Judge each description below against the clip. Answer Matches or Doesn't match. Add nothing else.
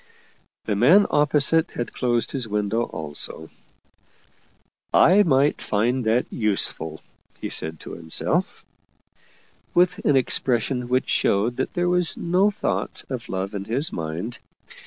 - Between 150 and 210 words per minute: Doesn't match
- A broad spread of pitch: Matches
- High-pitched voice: Doesn't match